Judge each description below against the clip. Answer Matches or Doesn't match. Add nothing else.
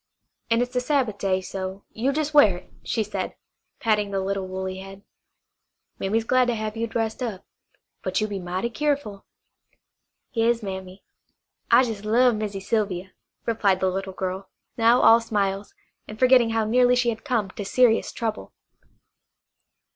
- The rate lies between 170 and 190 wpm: Doesn't match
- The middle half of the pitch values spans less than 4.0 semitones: Matches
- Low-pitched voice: Doesn't match